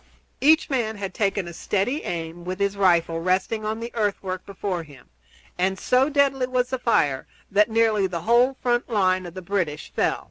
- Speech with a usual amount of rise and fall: Yes, average, 4.6 semitones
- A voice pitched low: No, high, 200 Hz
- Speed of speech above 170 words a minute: Yes, average, 185 wpm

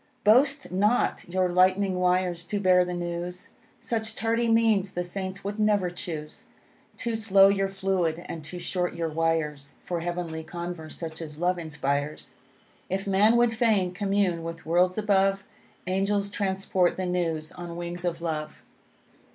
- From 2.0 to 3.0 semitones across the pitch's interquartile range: Yes, average, 2.7 semitones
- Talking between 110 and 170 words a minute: Yes, average, 150 wpm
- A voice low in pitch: No, medium, 180 Hz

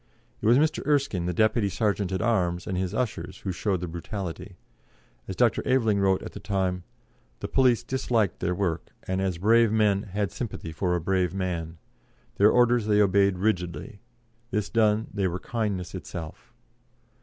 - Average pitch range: Yes, average, 3.4 semitones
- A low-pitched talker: Yes, low, 100 Hz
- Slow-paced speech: No, average, 175 wpm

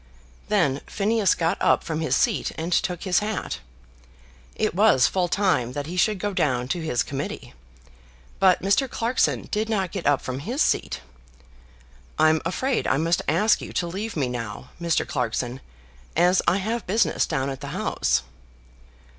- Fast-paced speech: No, average, 165 wpm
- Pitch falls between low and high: Yes, medium, 175 Hz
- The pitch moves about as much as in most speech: No, wide, 6.8 semitones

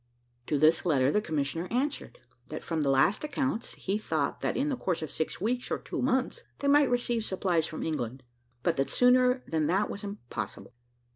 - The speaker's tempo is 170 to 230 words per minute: Yes, average, 195 wpm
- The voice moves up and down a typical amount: No, wide, 8.1 semitones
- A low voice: No, high, 195 Hz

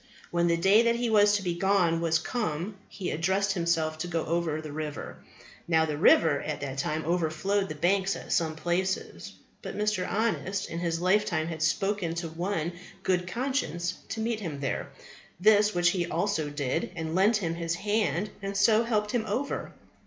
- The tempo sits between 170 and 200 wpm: Yes, average, 185 wpm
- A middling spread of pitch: Yes, average, 4.0 semitones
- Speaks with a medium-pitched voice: Yes, medium, 175 Hz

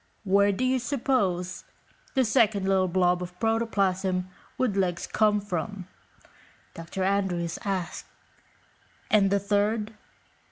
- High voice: Yes, high, 195 Hz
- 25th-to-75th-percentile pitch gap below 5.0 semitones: Yes, average, 2.8 semitones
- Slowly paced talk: Yes, slow, 115 wpm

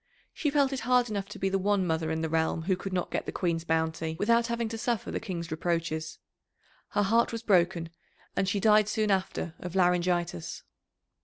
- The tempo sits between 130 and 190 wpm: No, fast, 205 wpm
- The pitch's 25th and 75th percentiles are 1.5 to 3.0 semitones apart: No, average, 4.4 semitones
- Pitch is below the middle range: No, medium, 185 Hz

